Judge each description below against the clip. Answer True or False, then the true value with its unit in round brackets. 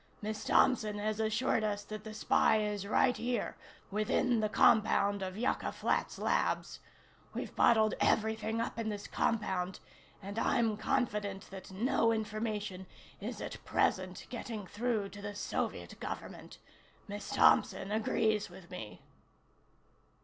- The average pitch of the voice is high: True (215 Hz)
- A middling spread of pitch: False (1.5 semitones)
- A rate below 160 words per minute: True (135 wpm)